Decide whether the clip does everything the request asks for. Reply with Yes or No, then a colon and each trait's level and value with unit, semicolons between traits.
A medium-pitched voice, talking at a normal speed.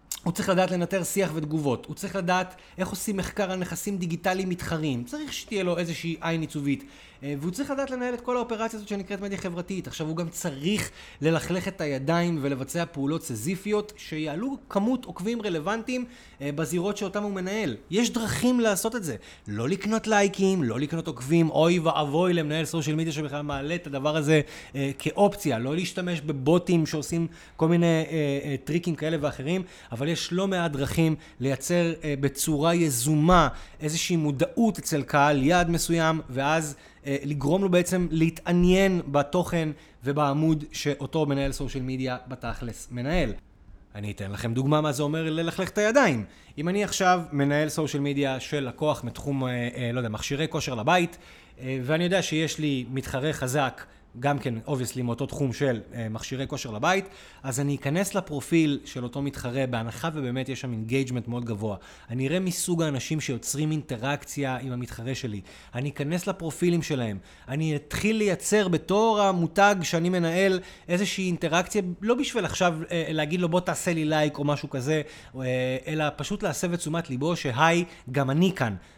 No: medium, 160 Hz; fast, 160 wpm